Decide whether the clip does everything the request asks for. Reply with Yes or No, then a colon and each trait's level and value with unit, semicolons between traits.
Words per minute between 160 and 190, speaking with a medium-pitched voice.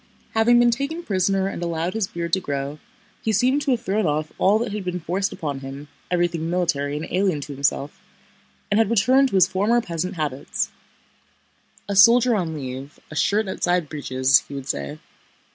Yes: average, 175 wpm; medium, 180 Hz